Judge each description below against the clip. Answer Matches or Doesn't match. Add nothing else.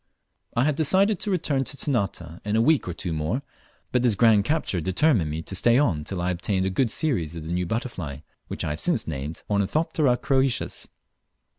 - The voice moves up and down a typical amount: Doesn't match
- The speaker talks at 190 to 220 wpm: Matches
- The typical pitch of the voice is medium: Doesn't match